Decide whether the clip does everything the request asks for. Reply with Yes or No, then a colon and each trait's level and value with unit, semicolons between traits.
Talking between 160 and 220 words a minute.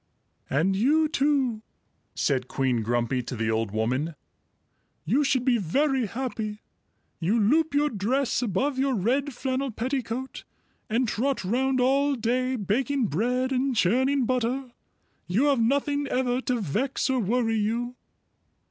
No: average, 140 wpm